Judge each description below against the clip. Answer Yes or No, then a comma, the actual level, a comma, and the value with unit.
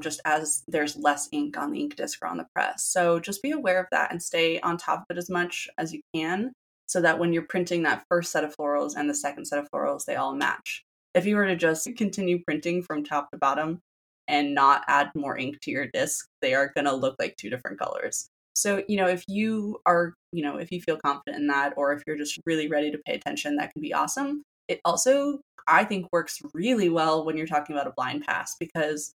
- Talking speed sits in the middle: No, fast, 245 wpm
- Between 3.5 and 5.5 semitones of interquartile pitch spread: Yes, average, 4.2 semitones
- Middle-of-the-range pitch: Yes, medium, 165 Hz